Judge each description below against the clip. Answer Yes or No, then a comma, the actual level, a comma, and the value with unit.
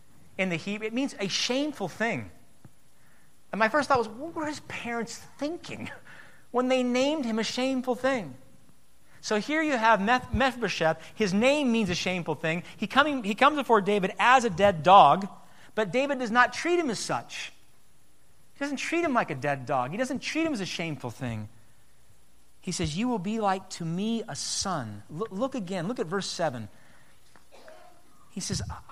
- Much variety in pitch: Yes, wide, 6.6 semitones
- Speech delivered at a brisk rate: No, average, 190 wpm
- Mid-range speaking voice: No, high, 220 Hz